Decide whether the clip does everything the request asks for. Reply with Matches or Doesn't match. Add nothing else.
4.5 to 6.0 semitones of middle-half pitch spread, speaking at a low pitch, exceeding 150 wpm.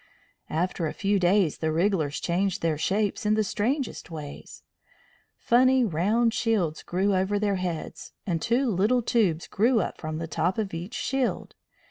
Doesn't match